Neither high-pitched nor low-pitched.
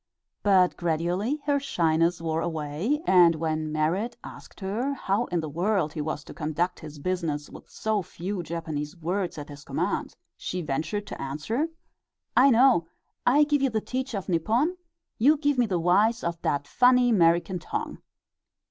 Yes: medium, 180 Hz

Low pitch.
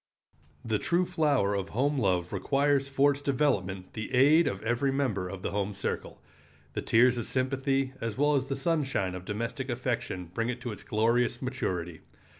Yes: low, 125 Hz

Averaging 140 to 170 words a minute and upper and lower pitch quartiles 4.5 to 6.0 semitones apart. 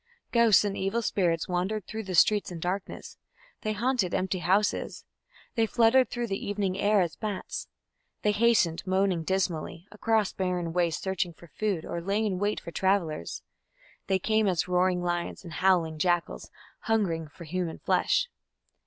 No: average, 160 wpm; average, 3.4 semitones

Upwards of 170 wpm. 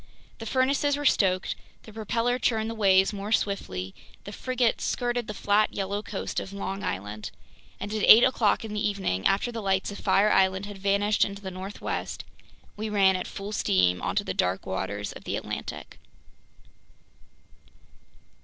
No: average, 165 wpm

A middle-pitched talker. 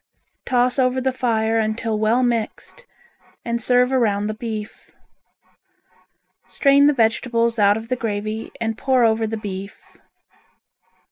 No: high, 230 Hz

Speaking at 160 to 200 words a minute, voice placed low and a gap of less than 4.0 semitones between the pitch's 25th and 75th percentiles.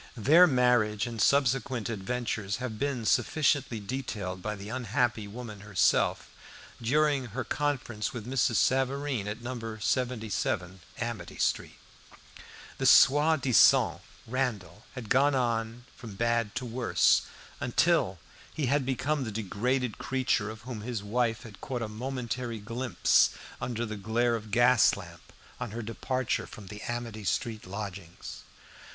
No: slow, 135 wpm; low, 120 Hz; average, 3.2 semitones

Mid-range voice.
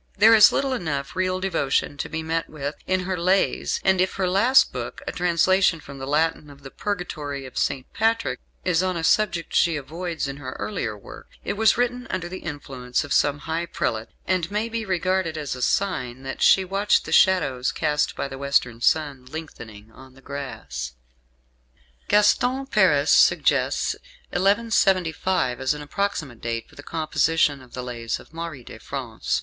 Yes: medium, 160 Hz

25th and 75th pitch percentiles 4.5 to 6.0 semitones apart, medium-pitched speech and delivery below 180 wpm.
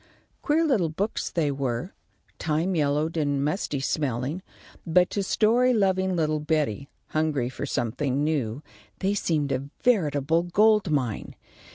Yes: average, 5.1 semitones; medium, 155 Hz; slow, 135 wpm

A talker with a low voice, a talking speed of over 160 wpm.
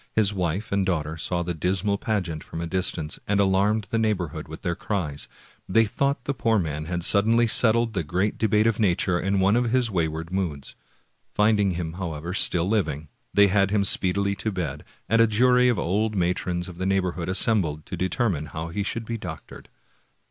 Yes: very low, 95 Hz; average, 190 wpm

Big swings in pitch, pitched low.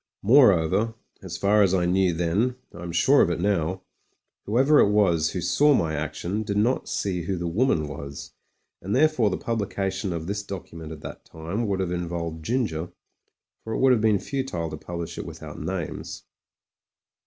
No: average, 4.4 semitones; very low, 95 Hz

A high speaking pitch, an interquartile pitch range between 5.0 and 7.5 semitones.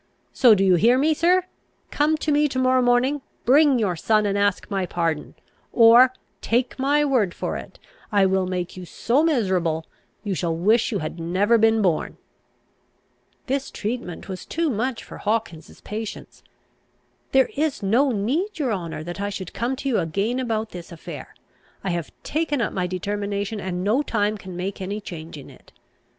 Yes: high, 210 Hz; wide, 5.6 semitones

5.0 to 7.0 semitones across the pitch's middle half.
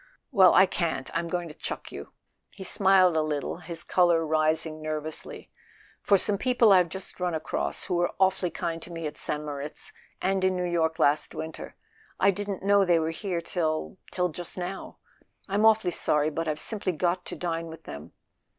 No: average, 3.0 semitones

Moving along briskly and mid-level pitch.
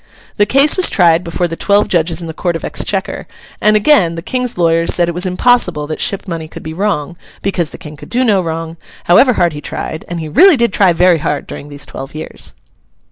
Yes: fast, 225 wpm; medium, 175 Hz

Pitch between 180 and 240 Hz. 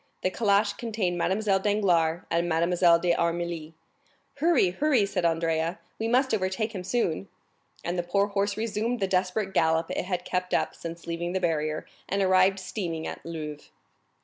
Yes: medium, 185 Hz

